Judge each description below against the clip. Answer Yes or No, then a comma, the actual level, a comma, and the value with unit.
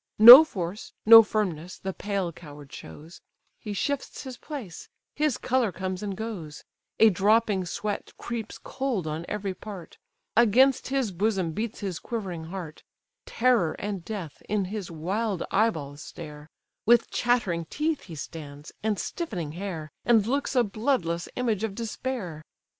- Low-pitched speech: No, high, 200 Hz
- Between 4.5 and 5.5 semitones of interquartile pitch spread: Yes, average, 5.2 semitones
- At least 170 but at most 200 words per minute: No, average, 145 wpm